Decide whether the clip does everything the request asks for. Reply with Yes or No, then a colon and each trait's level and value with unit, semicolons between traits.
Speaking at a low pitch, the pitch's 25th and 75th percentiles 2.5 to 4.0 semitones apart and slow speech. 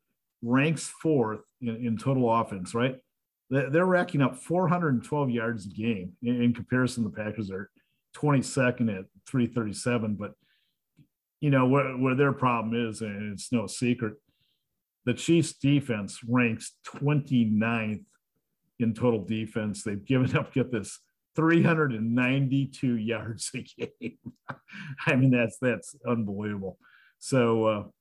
Yes: low, 120 Hz; average, 3.5 semitones; slow, 130 wpm